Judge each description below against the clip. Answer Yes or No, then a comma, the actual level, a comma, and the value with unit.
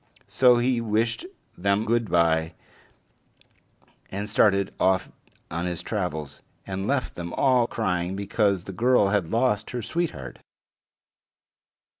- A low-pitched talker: Yes, low, 100 Hz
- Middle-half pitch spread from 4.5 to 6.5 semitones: Yes, average, 4.8 semitones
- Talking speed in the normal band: No, slow, 120 wpm